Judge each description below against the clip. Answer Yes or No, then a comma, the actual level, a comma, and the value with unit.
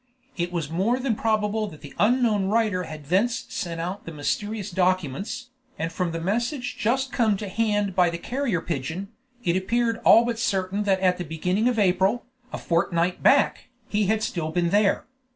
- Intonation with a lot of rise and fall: No, average, 4.3 semitones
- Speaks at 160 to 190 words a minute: Yes, average, 185 wpm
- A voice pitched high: Yes, high, 195 Hz